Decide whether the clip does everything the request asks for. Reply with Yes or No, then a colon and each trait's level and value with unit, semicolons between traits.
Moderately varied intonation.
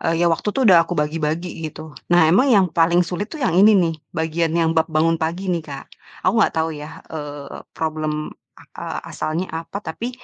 No: narrow, 2.1 semitones